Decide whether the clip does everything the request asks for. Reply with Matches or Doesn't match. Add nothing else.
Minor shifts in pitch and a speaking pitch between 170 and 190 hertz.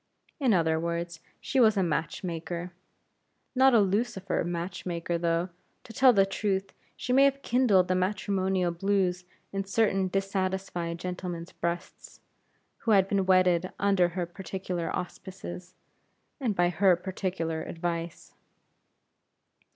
Matches